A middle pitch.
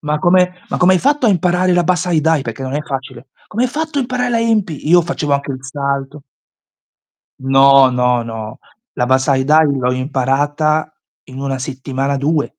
Yes: medium, 145 Hz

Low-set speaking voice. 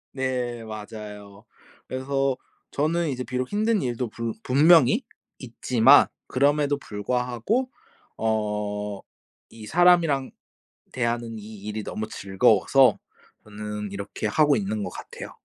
Yes: low, 120 Hz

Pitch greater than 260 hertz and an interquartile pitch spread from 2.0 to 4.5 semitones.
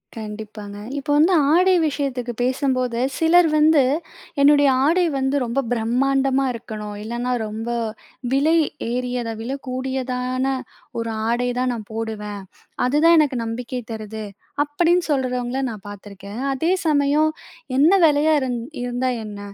No: very high, 255 Hz; average, 3.9 semitones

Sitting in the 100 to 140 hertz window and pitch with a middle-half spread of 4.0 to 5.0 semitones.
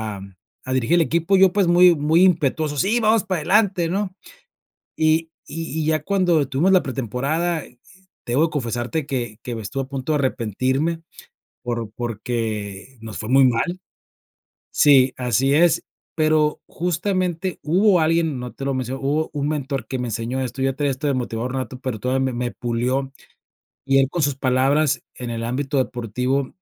Yes: low, 135 Hz; average, 4.5 semitones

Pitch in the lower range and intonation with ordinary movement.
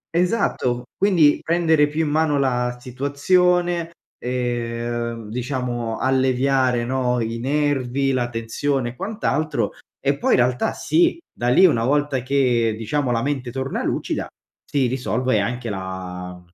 Yes: low, 130 Hz; average, 3.5 semitones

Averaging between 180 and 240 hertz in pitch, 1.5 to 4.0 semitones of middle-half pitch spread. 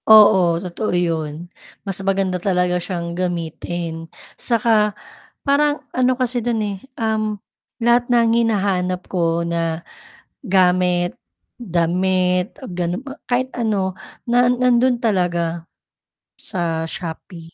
No: medium, 185 Hz; average, 4.6 semitones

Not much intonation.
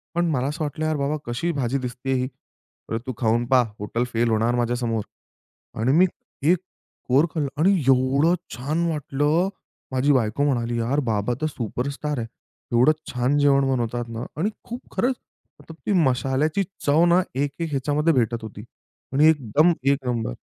No: average, 4.0 semitones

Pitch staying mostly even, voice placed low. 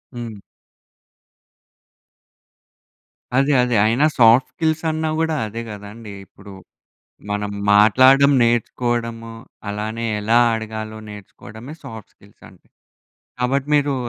No: average, 3.8 semitones; low, 115 Hz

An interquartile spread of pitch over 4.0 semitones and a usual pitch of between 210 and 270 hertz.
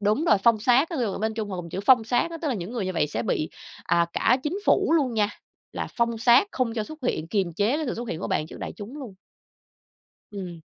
Yes: average, 4.5 semitones; high, 220 Hz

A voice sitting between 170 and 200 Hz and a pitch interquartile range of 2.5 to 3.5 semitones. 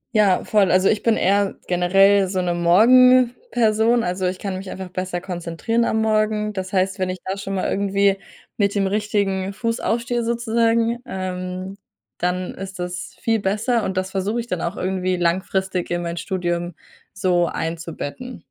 Yes: high, 190 Hz; average, 3.0 semitones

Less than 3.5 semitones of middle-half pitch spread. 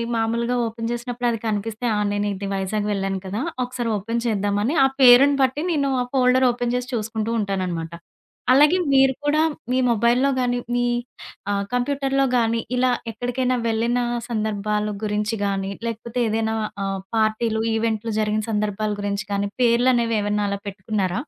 Yes: average, 3.0 semitones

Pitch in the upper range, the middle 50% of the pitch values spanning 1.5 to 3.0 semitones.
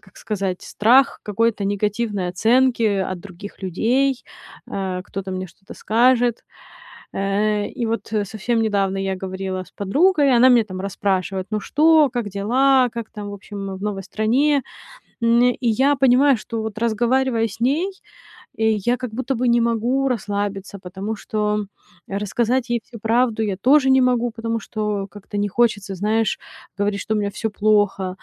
No: high, 215 Hz; average, 3.4 semitones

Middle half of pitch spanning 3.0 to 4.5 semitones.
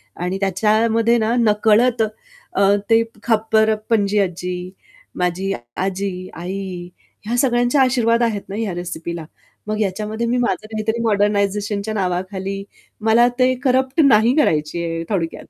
Yes: average, 3.5 semitones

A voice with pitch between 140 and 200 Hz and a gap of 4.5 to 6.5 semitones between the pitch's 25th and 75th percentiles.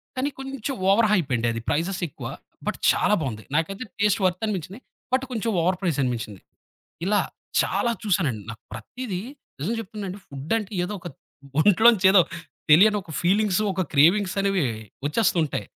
Yes: high, 190 Hz; average, 5.3 semitones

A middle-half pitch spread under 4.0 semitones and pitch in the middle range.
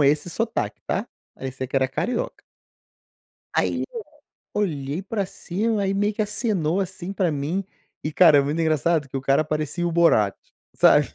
No: wide, 5.5 semitones; medium, 165 Hz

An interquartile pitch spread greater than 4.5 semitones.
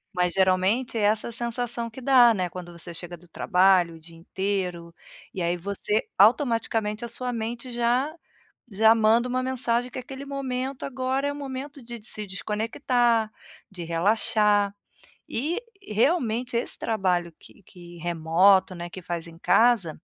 Yes: average, 5.3 semitones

